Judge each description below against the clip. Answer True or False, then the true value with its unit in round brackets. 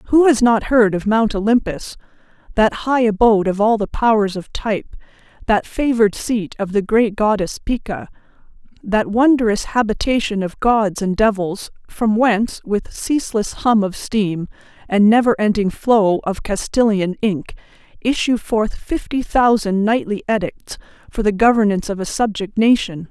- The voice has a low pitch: False (215 Hz)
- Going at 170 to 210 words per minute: False (150 wpm)